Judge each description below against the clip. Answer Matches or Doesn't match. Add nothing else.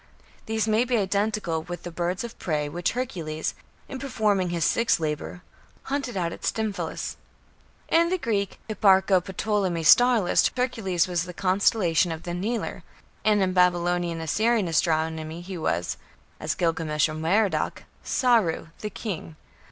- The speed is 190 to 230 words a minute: Doesn't match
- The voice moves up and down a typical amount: Matches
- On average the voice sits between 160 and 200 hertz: Matches